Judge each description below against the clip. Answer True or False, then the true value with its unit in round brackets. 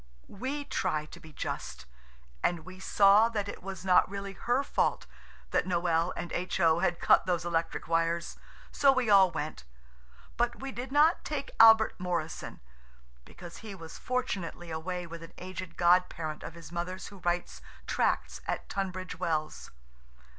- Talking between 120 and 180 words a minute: True (160 wpm)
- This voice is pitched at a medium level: True (180 Hz)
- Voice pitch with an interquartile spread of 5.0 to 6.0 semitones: False (3.4 semitones)